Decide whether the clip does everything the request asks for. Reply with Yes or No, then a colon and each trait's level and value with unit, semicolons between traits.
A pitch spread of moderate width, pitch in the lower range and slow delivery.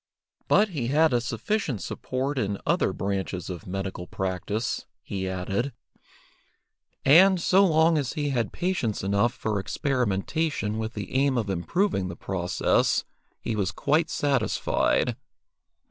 No: wide, 7.1 semitones; low, 115 Hz; slow, 130 wpm